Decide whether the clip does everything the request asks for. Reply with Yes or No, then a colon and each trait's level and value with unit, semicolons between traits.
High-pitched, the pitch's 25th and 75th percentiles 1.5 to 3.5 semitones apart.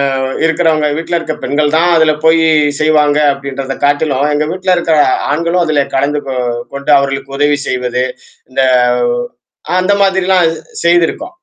No: medium, 155 Hz; average, 3.2 semitones